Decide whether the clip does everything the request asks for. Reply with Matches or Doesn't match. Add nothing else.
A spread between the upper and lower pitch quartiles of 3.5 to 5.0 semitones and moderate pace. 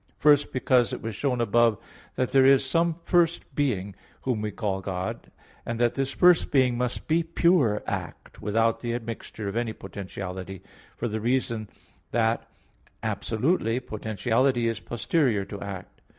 Matches